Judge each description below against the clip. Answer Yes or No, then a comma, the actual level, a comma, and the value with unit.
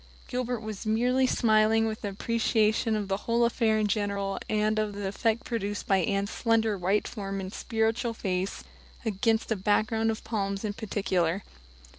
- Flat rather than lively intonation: Yes, narrow, 2.1 semitones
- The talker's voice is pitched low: No, high, 215 Hz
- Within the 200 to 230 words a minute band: No, average, 160 wpm